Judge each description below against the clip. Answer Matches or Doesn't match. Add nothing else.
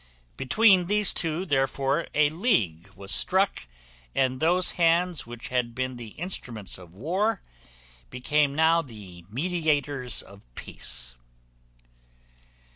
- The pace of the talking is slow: Matches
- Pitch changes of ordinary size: Doesn't match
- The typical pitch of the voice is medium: Matches